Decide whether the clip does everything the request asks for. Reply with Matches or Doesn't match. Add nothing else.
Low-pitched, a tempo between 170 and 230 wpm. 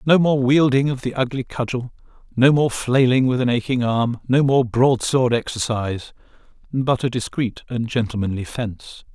Doesn't match